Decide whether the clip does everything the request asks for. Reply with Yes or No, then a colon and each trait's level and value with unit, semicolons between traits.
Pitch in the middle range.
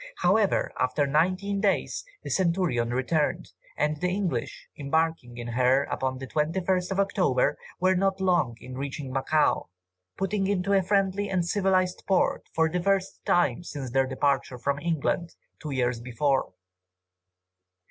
Yes: medium, 160 Hz